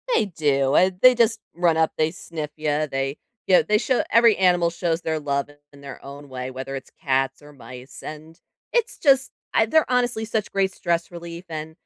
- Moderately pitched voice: Yes, medium, 160 Hz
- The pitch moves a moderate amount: No, wide, 5.7 semitones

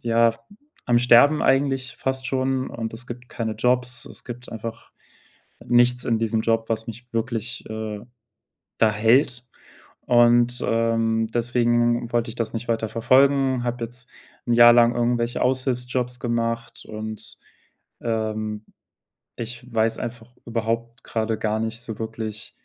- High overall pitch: No, low, 120 Hz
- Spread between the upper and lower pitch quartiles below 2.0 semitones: Yes, narrow, 1.5 semitones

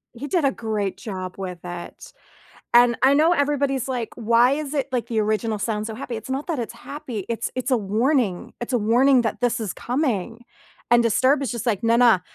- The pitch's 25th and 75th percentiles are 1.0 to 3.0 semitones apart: No, average, 3.5 semitones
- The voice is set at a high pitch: Yes, high, 235 Hz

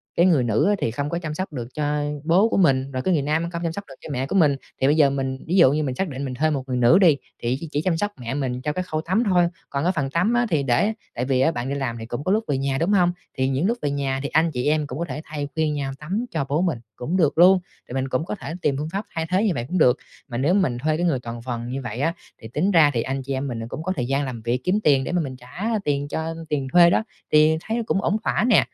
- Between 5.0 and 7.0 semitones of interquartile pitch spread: No, average, 4.6 semitones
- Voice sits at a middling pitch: Yes, medium, 150 Hz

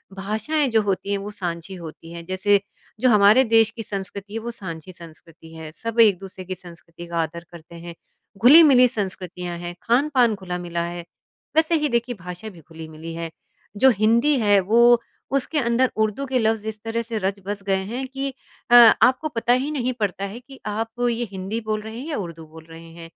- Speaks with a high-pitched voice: Yes, high, 205 Hz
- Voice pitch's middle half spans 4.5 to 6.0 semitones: Yes, wide, 5.4 semitones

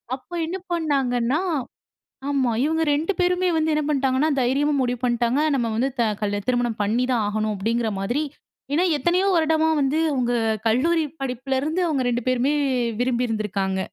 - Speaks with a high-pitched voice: Yes, very high, 260 Hz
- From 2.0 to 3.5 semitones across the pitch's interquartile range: No, average, 4.6 semitones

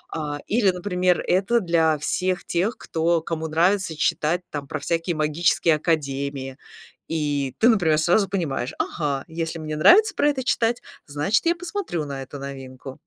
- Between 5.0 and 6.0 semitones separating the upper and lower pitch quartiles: No, average, 4.3 semitones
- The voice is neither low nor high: Yes, medium, 165 Hz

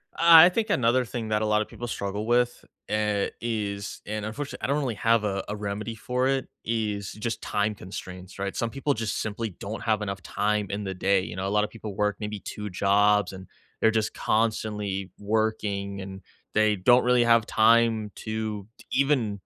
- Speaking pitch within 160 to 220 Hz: No, low, 105 Hz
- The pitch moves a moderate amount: No, narrow, 2.2 semitones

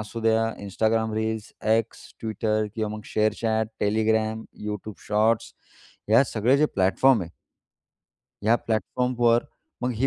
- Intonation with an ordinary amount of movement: No, narrow, 1.1 semitones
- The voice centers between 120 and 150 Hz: No, low, 110 Hz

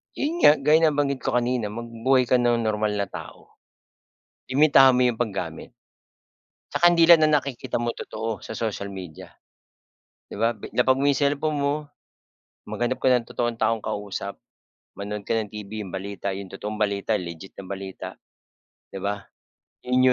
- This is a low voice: Yes, low, 115 Hz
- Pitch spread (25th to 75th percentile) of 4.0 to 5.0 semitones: Yes, average, 4.6 semitones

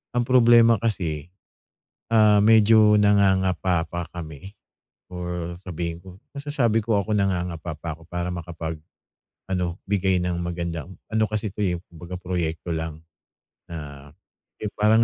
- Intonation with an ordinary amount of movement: Yes, average, 3.8 semitones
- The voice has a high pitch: No, very low, 90 Hz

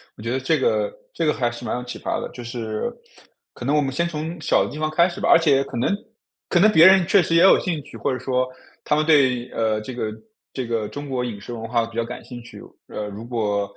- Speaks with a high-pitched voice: No, low, 130 Hz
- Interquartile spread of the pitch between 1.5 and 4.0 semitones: No, average, 5.1 semitones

